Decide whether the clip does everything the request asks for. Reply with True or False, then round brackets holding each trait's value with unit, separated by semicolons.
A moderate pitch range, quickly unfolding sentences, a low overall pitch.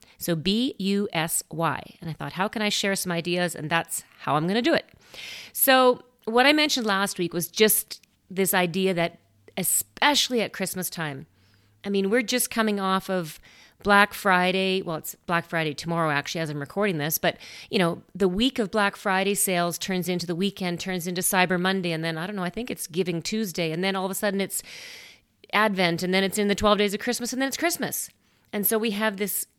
False (3.4 semitones; 220 wpm; 190 Hz)